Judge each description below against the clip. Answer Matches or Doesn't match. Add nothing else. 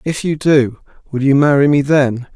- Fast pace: Doesn't match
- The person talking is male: Matches